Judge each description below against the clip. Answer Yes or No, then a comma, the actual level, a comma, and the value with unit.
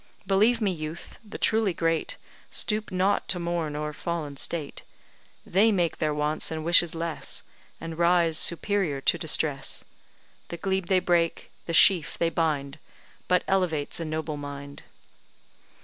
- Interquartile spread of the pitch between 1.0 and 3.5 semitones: Yes, average, 3.0 semitones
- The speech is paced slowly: No, average, 145 wpm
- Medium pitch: Yes, medium, 165 Hz